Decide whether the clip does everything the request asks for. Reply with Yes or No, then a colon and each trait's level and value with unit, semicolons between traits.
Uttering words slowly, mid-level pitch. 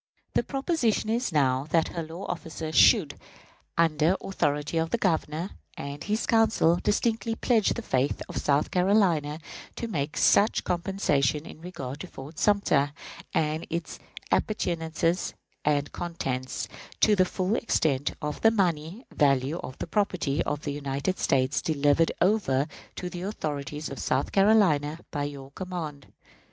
No: average, 145 wpm; medium, 160 Hz